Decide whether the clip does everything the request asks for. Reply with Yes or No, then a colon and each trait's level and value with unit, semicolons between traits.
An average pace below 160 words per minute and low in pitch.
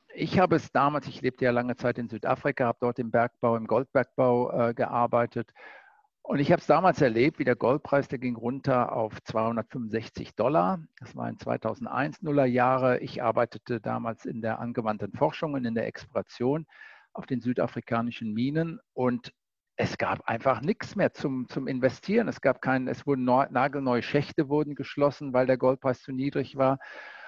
No: average, 175 wpm; low, 125 Hz